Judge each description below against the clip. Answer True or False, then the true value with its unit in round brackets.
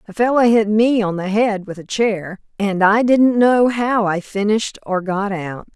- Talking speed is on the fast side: True (210 wpm)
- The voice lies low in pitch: False (210 Hz)